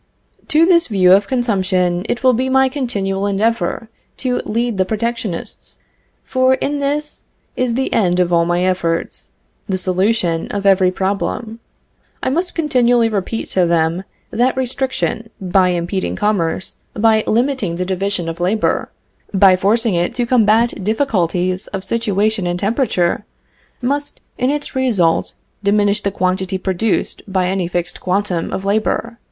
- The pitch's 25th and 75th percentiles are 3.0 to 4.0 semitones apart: No, average, 4.5 semitones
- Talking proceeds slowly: No, average, 145 wpm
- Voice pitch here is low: No, high, 205 Hz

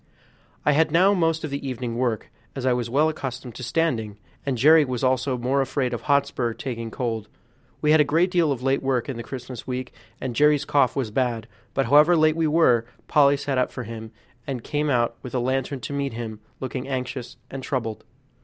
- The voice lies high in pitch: No, low, 130 Hz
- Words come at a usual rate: No, fast, 210 wpm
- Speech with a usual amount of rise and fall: Yes, average, 3.2 semitones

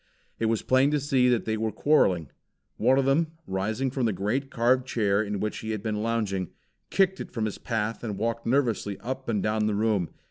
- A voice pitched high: No, low, 115 Hz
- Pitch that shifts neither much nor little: Yes, average, 3.6 semitones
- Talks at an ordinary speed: No, fast, 215 wpm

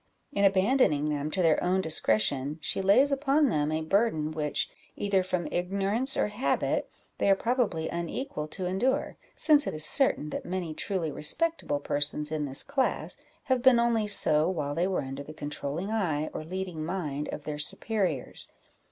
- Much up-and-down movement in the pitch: Yes, wide, 5.7 semitones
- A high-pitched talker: No, medium, 180 Hz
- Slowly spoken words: No, average, 170 wpm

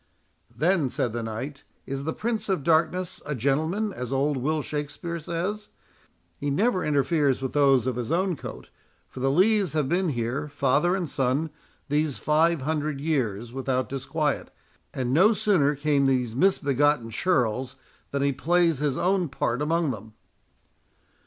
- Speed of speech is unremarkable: Yes, average, 155 wpm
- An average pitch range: Yes, average, 4.2 semitones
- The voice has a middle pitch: Yes, medium, 145 Hz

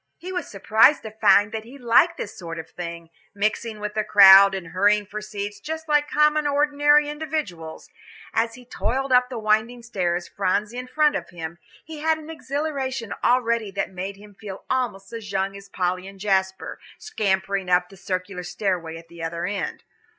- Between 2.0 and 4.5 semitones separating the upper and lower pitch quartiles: No, average, 4.9 semitones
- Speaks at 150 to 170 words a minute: No, average, 185 wpm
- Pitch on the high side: Yes, high, 210 Hz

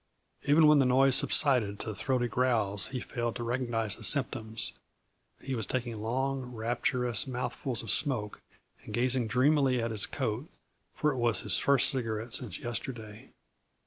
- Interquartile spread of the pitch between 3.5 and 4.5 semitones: No, average, 2.8 semitones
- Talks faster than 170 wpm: No, average, 155 wpm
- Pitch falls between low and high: No, low, 125 Hz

